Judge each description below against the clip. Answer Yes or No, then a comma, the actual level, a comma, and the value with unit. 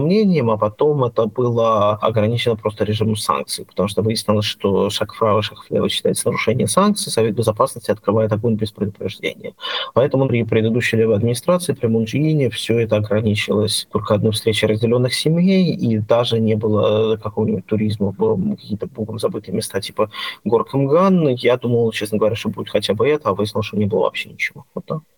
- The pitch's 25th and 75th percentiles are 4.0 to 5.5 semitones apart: No, narrow, 2.4 semitones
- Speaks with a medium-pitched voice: No, low, 110 Hz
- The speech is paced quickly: Yes, fast, 165 wpm